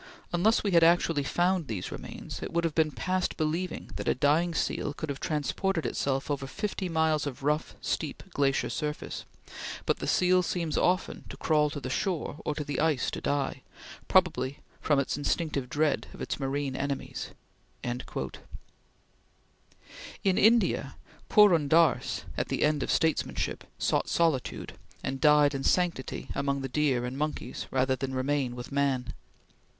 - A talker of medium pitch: Yes, medium, 150 Hz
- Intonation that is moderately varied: Yes, average, 3.5 semitones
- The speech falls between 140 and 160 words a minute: Yes, average, 155 wpm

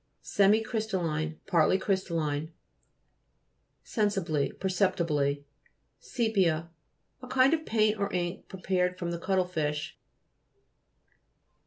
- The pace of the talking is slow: Yes, slow, 100 wpm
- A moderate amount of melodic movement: Yes, average, 4.4 semitones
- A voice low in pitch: No, medium, 180 Hz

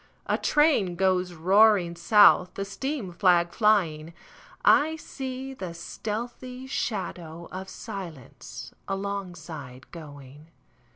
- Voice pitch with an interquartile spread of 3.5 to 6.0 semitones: Yes, average, 4.4 semitones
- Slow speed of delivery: Yes, slow, 80 wpm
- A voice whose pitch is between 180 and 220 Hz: Yes, high, 190 Hz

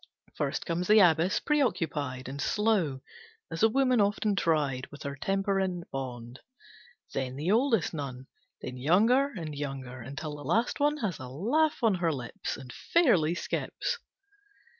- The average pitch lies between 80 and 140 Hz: No, medium, 165 Hz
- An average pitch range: No, wide, 7.9 semitones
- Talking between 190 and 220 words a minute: No, average, 155 wpm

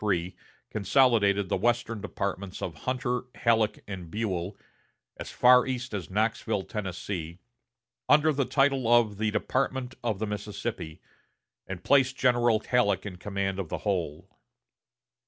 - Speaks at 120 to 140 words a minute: Yes, slow, 135 wpm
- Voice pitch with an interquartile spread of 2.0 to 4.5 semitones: Yes, average, 4.0 semitones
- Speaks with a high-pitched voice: No, low, 105 Hz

